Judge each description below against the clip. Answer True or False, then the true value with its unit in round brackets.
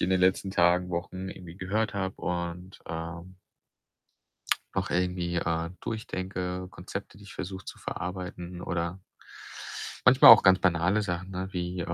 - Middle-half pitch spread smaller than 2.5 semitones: True (1.4 semitones)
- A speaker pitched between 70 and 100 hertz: True (90 Hz)